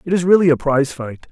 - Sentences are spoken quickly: Yes, fast, 275 wpm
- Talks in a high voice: No, medium, 155 Hz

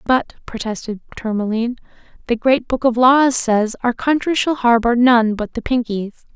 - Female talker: Yes, female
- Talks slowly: No, average, 160 wpm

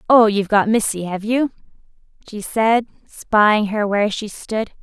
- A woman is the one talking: Yes, female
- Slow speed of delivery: No, average, 160 wpm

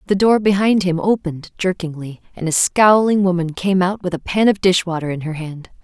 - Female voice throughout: Yes, female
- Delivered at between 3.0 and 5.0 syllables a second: No, 5.4 syllables/s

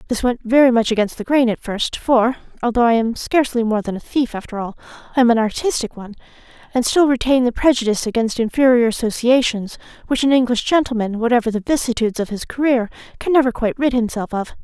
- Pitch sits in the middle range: No, high, 240 Hz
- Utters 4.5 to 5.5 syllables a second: No, 6.5 syllables/s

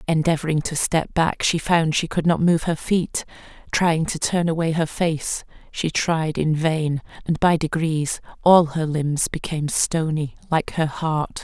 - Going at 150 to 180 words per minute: Yes, average, 175 wpm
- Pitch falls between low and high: Yes, medium, 160 Hz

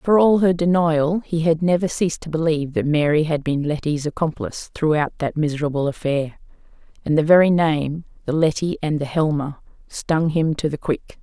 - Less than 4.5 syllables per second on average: No, 5.2 syllables/s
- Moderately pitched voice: Yes, medium, 155 Hz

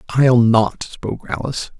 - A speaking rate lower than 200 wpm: Yes, slow, 135 wpm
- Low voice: Yes, low, 120 Hz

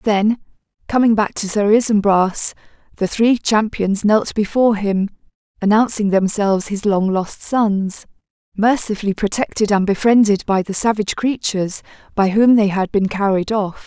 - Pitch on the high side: Yes, high, 205 Hz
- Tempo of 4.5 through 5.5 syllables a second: Yes, 4.8 syllables/s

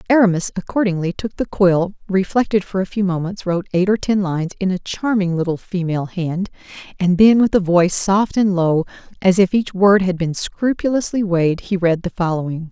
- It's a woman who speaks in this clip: Yes, female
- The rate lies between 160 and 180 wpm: No, average, 195 wpm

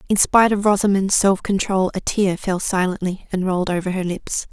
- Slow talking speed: No, average, 200 wpm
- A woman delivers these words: Yes, female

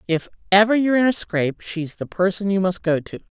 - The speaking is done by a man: No, female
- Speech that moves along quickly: Yes, fast, 230 wpm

